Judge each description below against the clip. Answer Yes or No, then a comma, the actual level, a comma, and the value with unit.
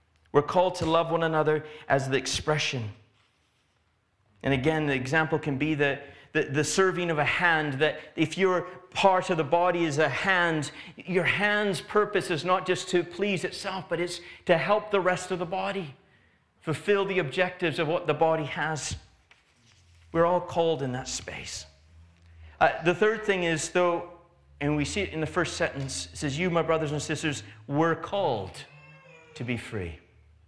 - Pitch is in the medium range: Yes, medium, 160 Hz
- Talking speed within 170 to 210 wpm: Yes, average, 175 wpm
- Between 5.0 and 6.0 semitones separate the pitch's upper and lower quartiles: Yes, wide, 5.4 semitones